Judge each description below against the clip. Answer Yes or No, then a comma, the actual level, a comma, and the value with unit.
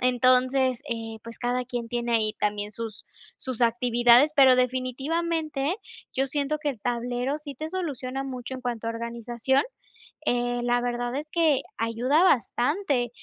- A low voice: No, very high, 250 Hz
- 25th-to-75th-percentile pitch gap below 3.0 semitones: Yes, narrow, 2.6 semitones